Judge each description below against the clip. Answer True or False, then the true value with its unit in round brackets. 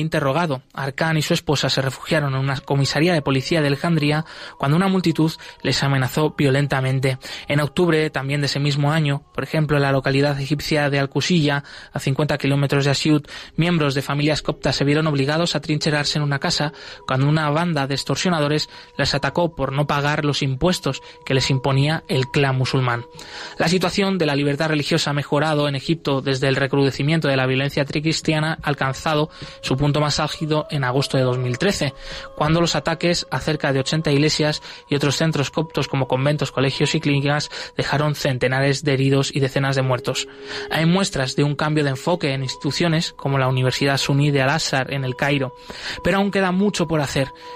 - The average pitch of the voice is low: False (145 Hz)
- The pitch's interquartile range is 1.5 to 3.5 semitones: True (2.4 semitones)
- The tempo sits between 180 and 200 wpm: True (185 wpm)